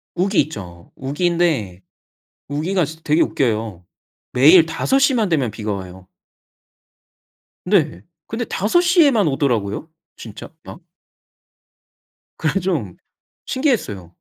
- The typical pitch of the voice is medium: Yes, medium, 155 Hz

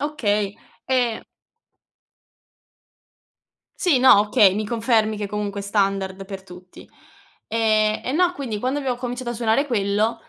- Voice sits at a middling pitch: No, high, 215 Hz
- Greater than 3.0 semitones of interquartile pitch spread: Yes, average, 3.6 semitones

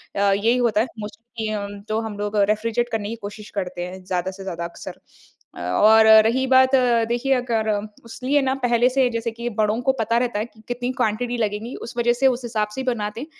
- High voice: Yes, high, 225 Hz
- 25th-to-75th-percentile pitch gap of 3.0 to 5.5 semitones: No, narrow, 2.6 semitones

